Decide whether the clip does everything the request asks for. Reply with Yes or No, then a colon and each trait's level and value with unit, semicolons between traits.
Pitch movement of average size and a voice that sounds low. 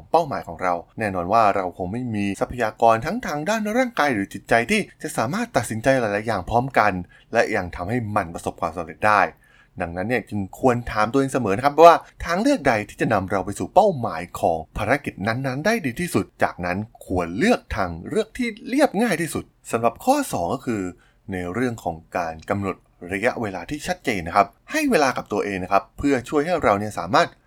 No: wide, 7.1 semitones; low, 115 Hz